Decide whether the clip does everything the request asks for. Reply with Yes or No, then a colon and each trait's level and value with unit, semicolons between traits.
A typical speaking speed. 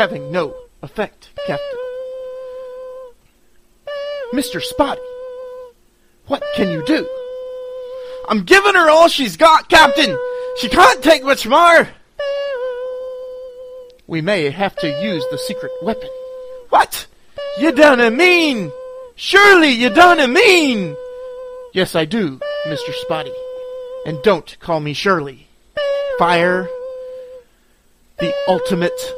No: slow, 105 wpm